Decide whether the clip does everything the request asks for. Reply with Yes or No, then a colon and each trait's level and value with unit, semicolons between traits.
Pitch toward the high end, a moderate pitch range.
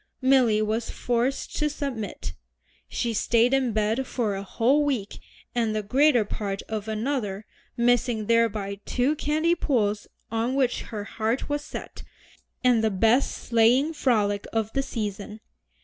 Yes: high, 230 Hz; average, 3.7 semitones